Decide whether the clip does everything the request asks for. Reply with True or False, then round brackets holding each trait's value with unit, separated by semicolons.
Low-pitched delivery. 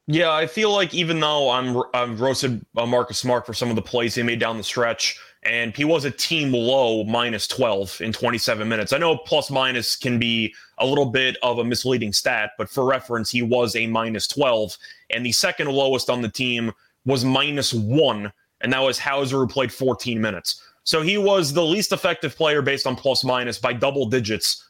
True (125 Hz)